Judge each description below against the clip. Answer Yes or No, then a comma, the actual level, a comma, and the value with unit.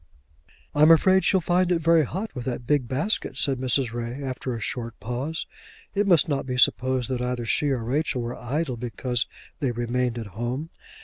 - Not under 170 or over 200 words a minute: Yes, average, 190 wpm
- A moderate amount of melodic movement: Yes, average, 4.3 semitones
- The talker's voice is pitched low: Yes, low, 130 Hz